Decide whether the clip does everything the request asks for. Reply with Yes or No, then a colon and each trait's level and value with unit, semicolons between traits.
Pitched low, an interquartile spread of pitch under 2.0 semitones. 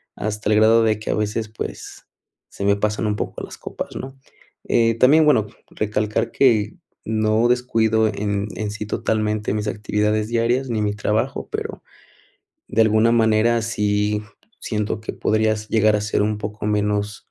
Yes: low, 110 Hz; narrow, 1.4 semitones